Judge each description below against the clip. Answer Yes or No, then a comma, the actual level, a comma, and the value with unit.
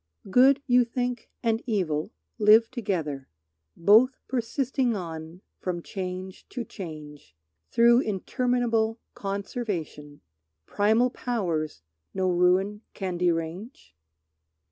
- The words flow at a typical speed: No, slow, 95 wpm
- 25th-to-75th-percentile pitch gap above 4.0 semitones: Yes, wide, 5.5 semitones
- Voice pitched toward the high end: Yes, high, 200 Hz